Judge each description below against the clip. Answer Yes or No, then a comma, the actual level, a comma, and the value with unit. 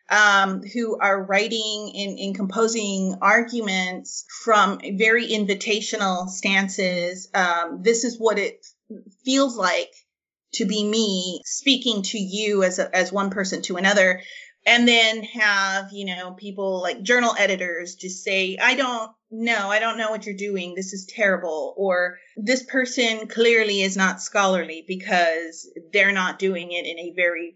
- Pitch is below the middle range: No, high, 200 Hz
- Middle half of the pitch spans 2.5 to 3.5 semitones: Yes, average, 3.1 semitones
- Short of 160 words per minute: Yes, average, 150 wpm